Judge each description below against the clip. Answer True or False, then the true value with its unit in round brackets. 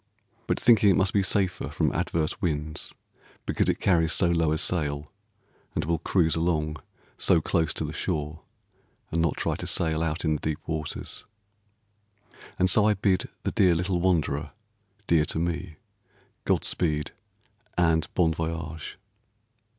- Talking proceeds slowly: False (155 wpm)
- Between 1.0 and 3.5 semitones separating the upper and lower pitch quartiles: True (2.4 semitones)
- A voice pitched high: False (80 Hz)